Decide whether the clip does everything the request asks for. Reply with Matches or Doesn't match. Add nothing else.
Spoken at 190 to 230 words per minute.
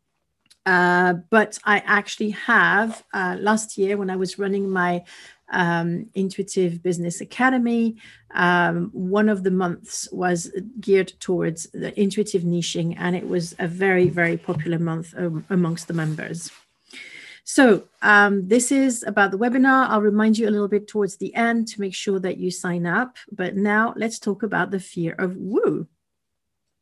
Doesn't match